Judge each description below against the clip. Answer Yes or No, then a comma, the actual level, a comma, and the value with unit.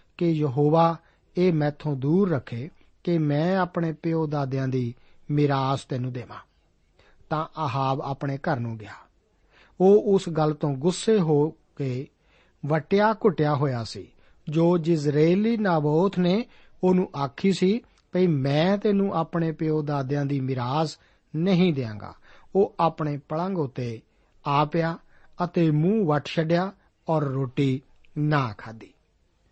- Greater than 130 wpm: No, average, 125 wpm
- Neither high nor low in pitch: Yes, medium, 155 Hz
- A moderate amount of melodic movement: Yes, average, 4.3 semitones